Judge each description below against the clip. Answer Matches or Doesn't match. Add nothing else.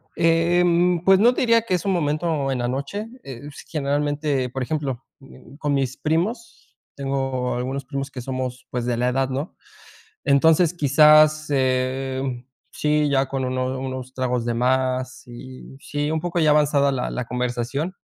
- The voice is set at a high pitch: Doesn't match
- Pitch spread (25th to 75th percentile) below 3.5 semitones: Matches